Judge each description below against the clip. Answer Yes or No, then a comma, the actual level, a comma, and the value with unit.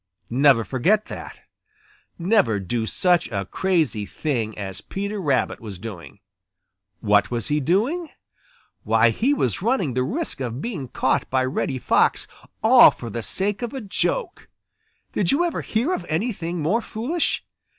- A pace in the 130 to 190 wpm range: Yes, average, 150 wpm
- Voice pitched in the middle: Yes, medium, 155 Hz